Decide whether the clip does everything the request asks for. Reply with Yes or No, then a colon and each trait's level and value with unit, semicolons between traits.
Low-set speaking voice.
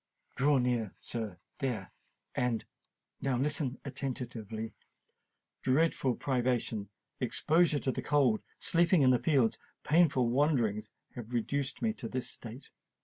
Yes: low, 125 Hz